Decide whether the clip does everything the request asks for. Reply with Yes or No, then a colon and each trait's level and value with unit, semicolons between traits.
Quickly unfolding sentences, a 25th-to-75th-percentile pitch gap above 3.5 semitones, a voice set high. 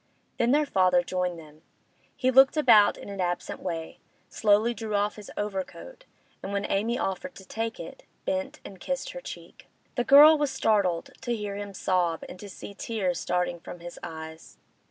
No: average, 180 wpm; average, 5.2 semitones; high, 205 Hz